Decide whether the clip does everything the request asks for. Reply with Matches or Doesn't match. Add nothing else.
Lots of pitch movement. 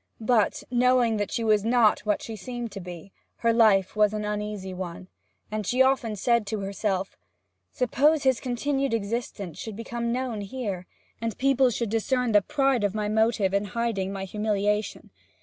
Doesn't match